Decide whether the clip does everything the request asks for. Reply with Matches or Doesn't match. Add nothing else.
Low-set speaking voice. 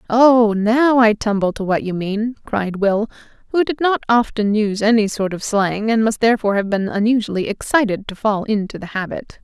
Doesn't match